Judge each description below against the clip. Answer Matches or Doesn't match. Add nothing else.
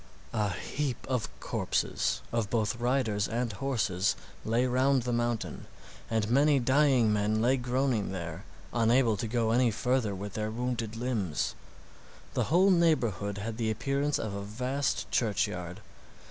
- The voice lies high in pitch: Doesn't match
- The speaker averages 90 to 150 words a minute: Matches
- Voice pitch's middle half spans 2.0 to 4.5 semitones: Matches